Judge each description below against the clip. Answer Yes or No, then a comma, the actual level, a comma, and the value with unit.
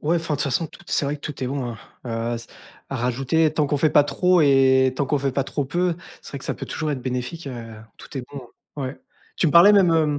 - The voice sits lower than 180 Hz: Yes, medium, 140 Hz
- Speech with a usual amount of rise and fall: Yes, average, 3.3 semitones